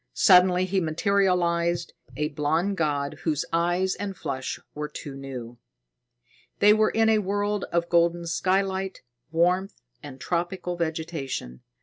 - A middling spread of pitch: Yes, average, 3.8 semitones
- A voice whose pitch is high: No, medium, 170 Hz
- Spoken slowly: Yes, slow, 125 wpm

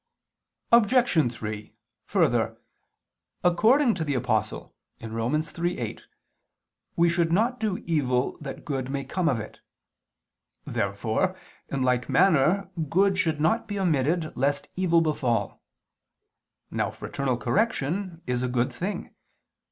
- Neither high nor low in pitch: Yes, medium, 155 Hz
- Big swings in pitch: Yes, wide, 6.6 semitones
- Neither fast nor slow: No, slow, 120 wpm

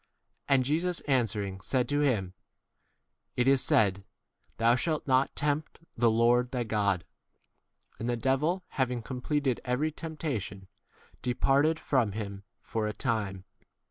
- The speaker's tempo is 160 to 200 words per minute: No, average, 140 wpm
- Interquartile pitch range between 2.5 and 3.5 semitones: No, average, 4.7 semitones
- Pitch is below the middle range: Yes, low, 125 Hz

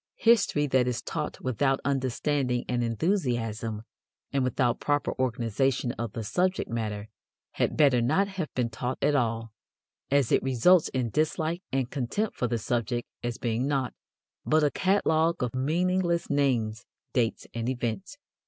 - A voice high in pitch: No, low, 130 Hz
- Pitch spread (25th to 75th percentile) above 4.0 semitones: Yes, average, 4.5 semitones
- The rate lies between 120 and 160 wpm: Yes, average, 150 wpm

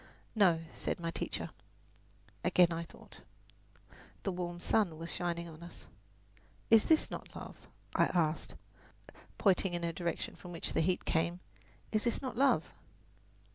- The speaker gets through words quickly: No, average, 145 wpm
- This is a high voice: No, medium, 175 Hz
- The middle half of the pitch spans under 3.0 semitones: Yes, narrow, 2.6 semitones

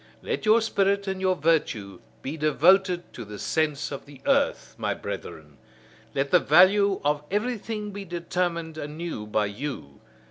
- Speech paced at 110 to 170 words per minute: Yes, average, 150 wpm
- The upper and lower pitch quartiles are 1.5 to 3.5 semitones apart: No, wide, 5.5 semitones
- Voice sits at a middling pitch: Yes, medium, 165 Hz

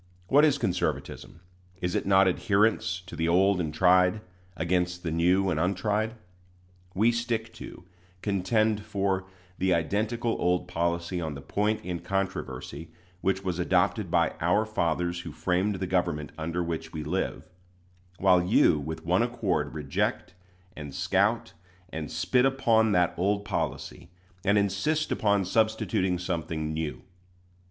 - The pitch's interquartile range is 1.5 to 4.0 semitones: Yes, average, 3.6 semitones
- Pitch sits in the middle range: No, very low, 95 Hz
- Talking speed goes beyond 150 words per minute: No, average, 140 wpm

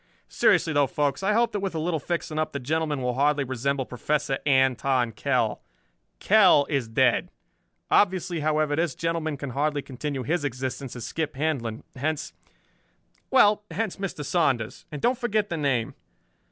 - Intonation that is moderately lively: Yes, average, 3.9 semitones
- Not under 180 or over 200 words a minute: No, average, 160 wpm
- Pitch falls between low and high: Yes, medium, 145 Hz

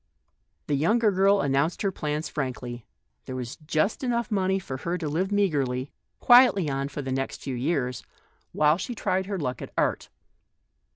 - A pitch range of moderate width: No, wide, 6.5 semitones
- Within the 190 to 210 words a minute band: No, average, 165 wpm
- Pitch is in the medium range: Yes, medium, 155 Hz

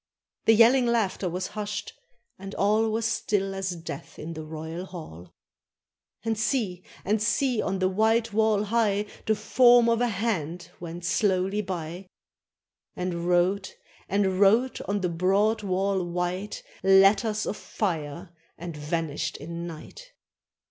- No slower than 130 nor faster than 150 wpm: Yes, average, 140 wpm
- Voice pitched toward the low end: No, high, 195 Hz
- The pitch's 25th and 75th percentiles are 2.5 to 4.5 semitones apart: Yes, average, 3.7 semitones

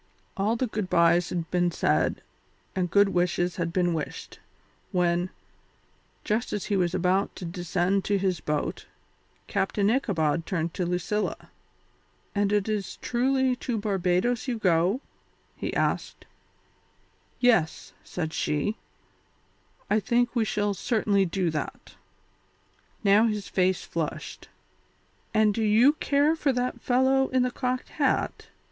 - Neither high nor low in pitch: No, high, 200 Hz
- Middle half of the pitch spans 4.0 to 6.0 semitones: Yes, average, 4.6 semitones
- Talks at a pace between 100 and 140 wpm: Yes, slow, 135 wpm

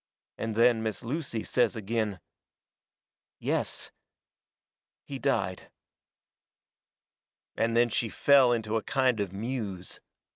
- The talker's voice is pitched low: Yes, low, 115 Hz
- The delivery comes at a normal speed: No, slow, 110 wpm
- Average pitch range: No, narrow, 2.2 semitones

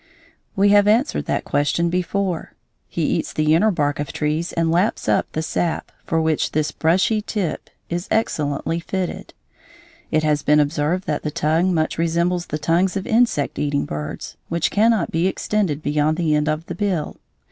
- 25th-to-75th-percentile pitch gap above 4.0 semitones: No, average, 3.4 semitones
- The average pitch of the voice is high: No, medium, 165 Hz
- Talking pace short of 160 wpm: No, average, 175 wpm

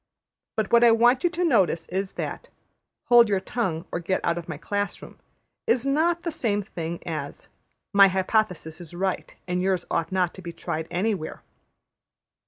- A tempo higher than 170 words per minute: Yes, average, 180 wpm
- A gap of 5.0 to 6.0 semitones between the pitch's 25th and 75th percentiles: Yes, average, 5.3 semitones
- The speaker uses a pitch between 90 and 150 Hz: No, high, 190 Hz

